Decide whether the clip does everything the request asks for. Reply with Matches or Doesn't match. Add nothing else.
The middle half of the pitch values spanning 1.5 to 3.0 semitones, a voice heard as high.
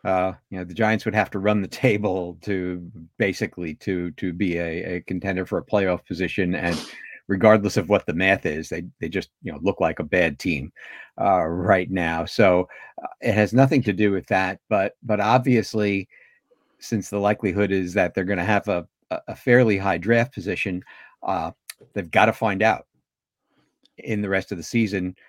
Doesn't match